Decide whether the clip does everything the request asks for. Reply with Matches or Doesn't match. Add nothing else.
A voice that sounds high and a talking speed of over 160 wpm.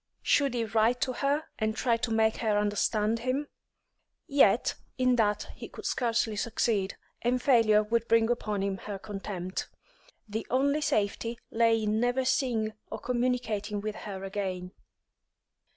Doesn't match